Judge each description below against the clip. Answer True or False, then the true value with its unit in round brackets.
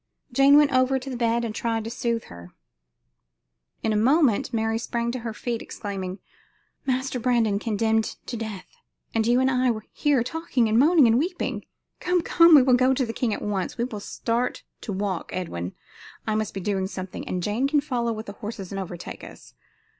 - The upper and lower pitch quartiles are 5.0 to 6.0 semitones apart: False (3.6 semitones)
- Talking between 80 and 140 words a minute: False (200 wpm)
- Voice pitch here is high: True (230 Hz)